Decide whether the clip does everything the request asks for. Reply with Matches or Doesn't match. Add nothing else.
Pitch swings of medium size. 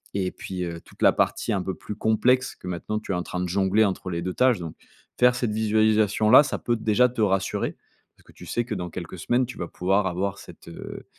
Matches